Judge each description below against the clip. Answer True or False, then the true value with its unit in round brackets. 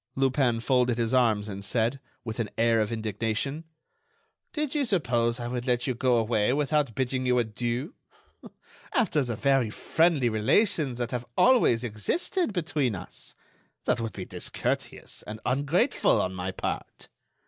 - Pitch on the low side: True (125 Hz)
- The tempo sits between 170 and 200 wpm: False (150 wpm)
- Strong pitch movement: False (3.8 semitones)